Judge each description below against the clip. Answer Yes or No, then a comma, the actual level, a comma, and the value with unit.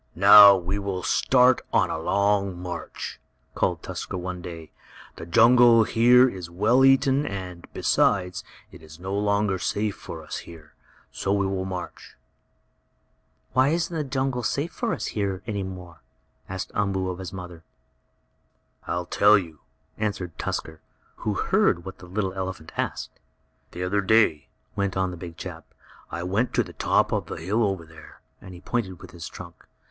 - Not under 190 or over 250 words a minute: No, average, 165 wpm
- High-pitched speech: No, very low, 95 Hz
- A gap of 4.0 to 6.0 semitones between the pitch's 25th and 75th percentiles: No, average, 3.2 semitones